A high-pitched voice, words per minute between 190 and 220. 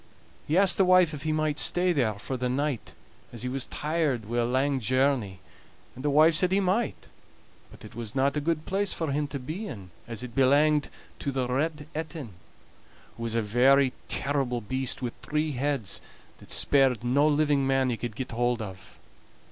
No: low, 135 Hz; average, 195 wpm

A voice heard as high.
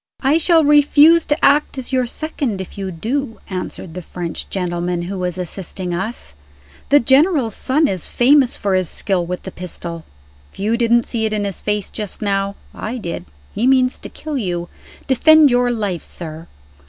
Yes: high, 215 Hz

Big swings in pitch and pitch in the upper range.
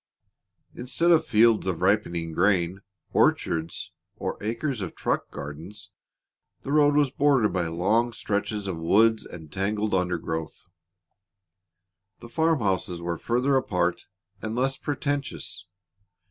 No: wide, 6.0 semitones; low, 105 Hz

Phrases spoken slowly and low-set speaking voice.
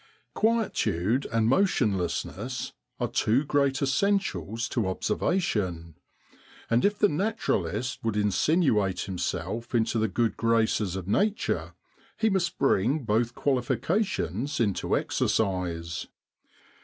Yes: slow, 105 wpm; low, 115 Hz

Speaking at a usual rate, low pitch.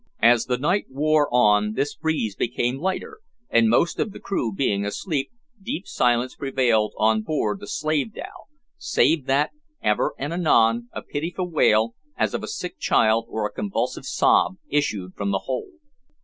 Yes: average, 165 wpm; low, 130 Hz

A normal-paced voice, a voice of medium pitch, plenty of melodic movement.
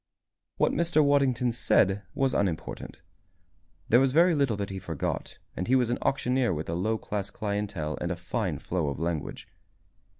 No: average, 170 wpm; low, 105 Hz; wide, 6.6 semitones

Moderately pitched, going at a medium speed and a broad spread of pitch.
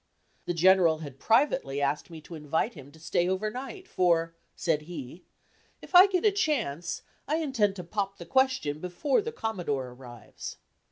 Yes: medium, 180 Hz; average, 170 wpm; wide, 9.0 semitones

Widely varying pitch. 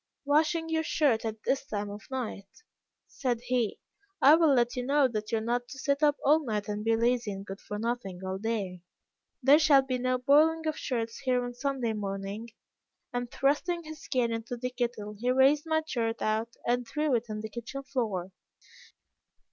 No: average, 4.1 semitones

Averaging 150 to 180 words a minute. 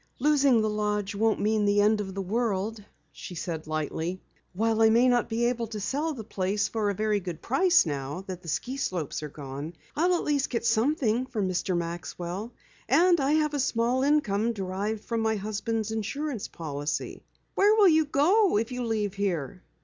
No: average, 190 wpm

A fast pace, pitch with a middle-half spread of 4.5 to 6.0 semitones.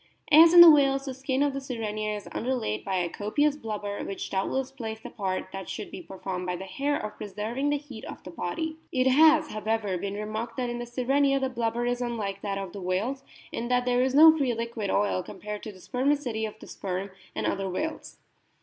Yes: fast, 230 wpm; average, 5.1 semitones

